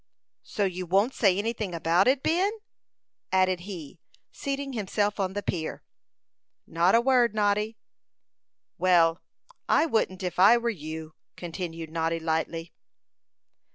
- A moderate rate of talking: No, slow, 125 wpm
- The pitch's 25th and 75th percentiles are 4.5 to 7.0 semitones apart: Yes, average, 4.9 semitones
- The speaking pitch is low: No, medium, 185 Hz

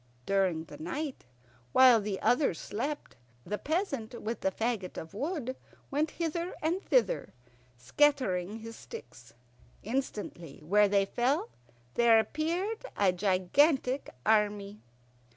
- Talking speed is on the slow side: Yes, slow, 115 wpm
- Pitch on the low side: No, high, 225 Hz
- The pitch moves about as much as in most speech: No, wide, 6.9 semitones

